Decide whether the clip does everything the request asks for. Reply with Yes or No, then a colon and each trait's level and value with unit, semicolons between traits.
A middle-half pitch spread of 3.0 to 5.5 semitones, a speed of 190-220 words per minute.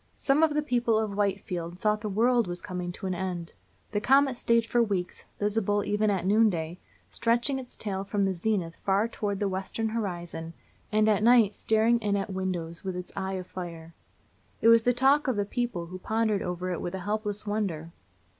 Yes: average, 3.6 semitones; average, 200 wpm